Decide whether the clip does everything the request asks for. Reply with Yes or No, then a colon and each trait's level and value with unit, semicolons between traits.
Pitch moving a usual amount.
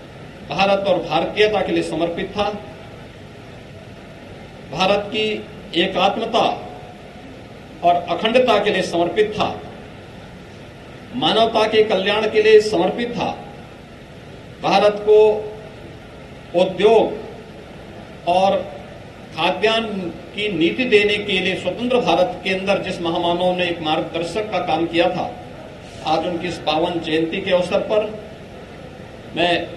Yes: average, 3.5 semitones